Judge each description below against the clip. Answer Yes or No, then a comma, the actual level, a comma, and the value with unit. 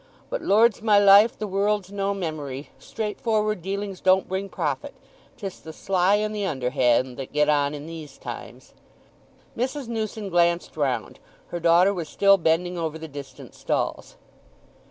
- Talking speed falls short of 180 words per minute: Yes, average, 140 wpm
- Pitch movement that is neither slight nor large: Yes, average, 4.7 semitones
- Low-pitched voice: No, high, 190 Hz